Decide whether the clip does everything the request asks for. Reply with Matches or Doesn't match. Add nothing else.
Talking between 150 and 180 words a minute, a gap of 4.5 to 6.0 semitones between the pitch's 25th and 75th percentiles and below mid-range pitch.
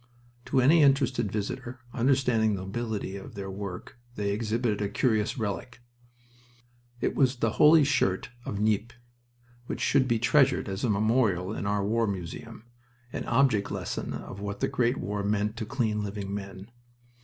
Doesn't match